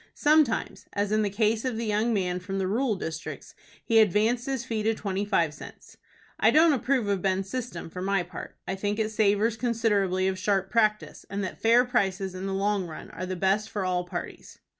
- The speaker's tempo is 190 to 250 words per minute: Yes, fast, 205 wpm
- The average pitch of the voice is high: Yes, high, 205 Hz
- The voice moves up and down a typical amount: Yes, average, 3.0 semitones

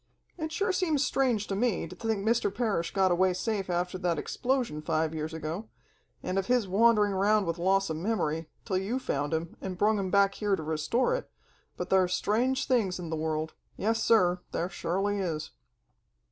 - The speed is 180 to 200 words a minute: Yes, average, 190 wpm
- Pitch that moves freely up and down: No, average, 4.8 semitones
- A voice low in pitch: No, high, 195 Hz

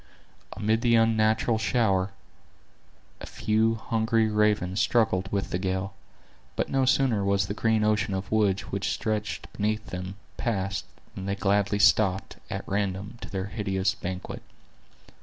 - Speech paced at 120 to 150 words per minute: Yes, average, 140 wpm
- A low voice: Yes, low, 105 Hz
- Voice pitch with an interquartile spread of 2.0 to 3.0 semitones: Yes, narrow, 2.4 semitones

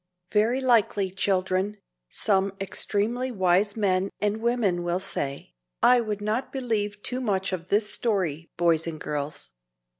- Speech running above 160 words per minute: No, average, 140 wpm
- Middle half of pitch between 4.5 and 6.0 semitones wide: No, average, 3.1 semitones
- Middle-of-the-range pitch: No, high, 200 Hz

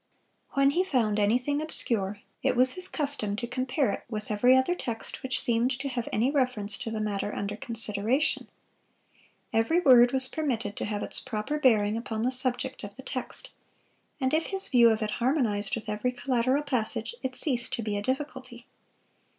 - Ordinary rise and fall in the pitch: Yes, average, 3.6 semitones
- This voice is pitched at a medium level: No, high, 245 Hz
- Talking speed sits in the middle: Yes, average, 185 wpm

